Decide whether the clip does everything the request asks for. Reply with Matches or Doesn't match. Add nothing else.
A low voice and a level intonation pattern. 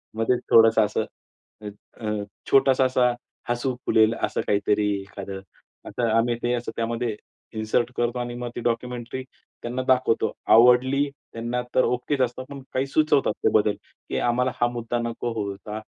Matches